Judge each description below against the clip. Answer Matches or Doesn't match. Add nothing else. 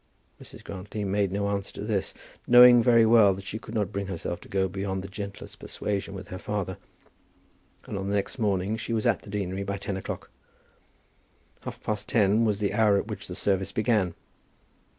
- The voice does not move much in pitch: Matches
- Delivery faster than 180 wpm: Matches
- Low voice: Matches